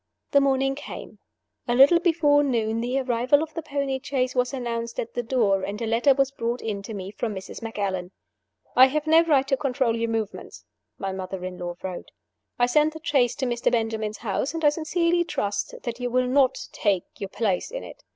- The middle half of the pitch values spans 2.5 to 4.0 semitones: No, average, 4.4 semitones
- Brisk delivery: Yes, fast, 210 wpm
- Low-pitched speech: No, high, 245 Hz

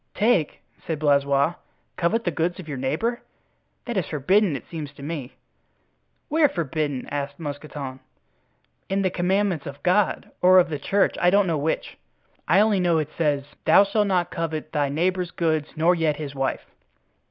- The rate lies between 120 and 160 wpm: No, average, 170 wpm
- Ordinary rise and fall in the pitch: Yes, average, 4.3 semitones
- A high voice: No, medium, 165 Hz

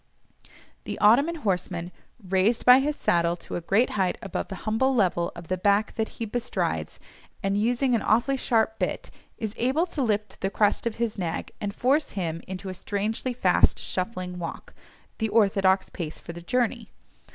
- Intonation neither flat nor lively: Yes, average, 4.4 semitones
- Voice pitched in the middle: No, high, 210 Hz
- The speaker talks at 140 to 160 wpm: No, average, 175 wpm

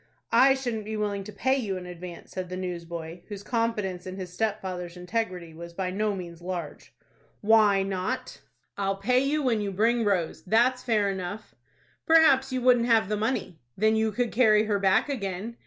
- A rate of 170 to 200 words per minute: Yes, average, 185 wpm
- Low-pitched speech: No, high, 205 Hz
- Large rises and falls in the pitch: No, average, 3.9 semitones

